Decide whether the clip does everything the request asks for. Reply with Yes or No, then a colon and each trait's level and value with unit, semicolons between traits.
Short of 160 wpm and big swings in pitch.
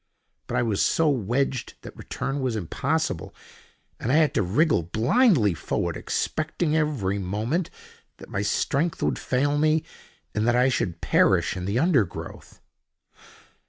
Yes: average, 145 wpm; wide, 7.0 semitones